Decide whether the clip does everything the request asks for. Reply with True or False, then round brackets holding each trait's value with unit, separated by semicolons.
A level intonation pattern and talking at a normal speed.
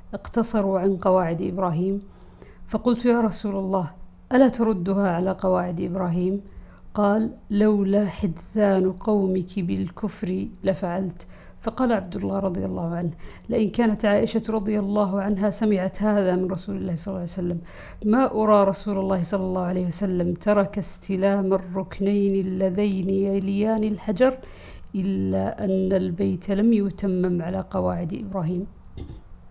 True (2.1 semitones; 125 wpm)